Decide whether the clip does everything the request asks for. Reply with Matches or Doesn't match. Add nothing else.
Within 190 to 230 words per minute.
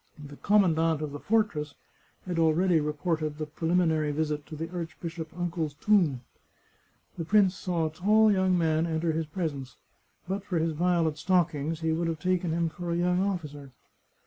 Doesn't match